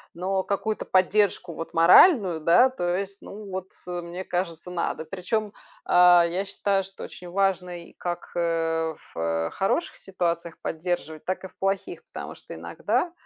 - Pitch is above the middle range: No, medium, 180 Hz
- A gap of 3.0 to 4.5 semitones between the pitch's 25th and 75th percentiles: No, narrow, 2.5 semitones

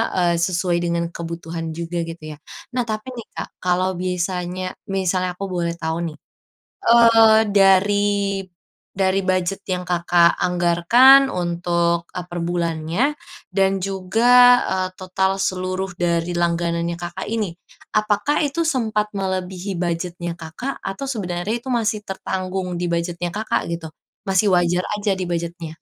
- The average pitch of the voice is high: No, medium, 180 Hz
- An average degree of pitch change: No, narrow, 2.2 semitones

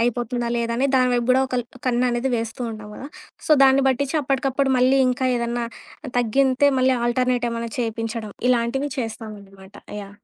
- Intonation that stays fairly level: Yes, narrow, 2.2 semitones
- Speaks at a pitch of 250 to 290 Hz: No, high, 240 Hz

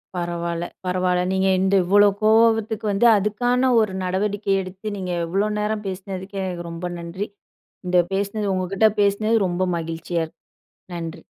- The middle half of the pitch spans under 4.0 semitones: Yes, average, 2.7 semitones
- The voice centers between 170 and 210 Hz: Yes, high, 190 Hz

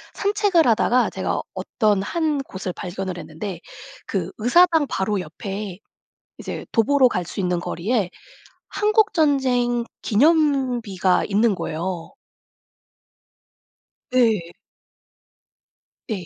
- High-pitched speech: Yes, high, 215 Hz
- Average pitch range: No, wide, 6.7 semitones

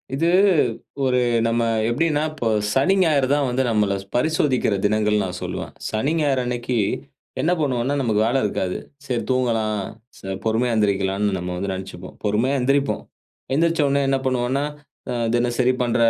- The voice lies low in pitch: Yes, low, 120 Hz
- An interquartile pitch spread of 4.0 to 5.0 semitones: Yes, average, 4.4 semitones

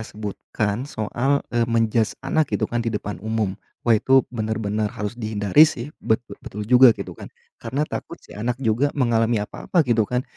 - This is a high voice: No, low, 115 Hz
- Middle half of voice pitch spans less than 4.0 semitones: Yes, average, 2.7 semitones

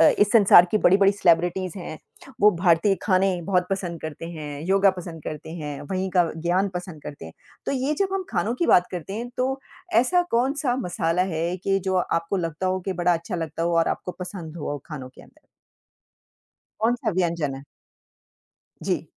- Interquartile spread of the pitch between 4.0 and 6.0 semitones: No, average, 3.1 semitones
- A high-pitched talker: No, medium, 180 Hz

